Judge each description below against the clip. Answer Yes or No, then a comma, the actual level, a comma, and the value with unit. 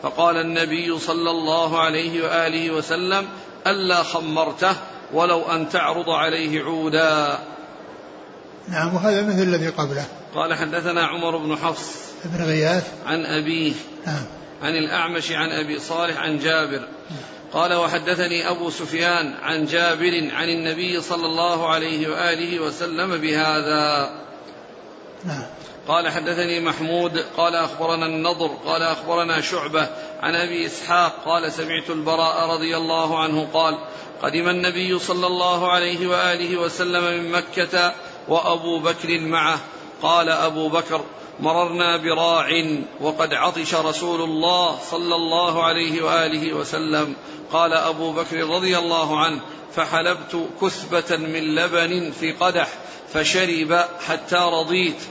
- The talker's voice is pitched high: No, medium, 165 Hz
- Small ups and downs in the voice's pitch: Yes, narrow, 1.3 semitones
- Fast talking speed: No, average, 120 wpm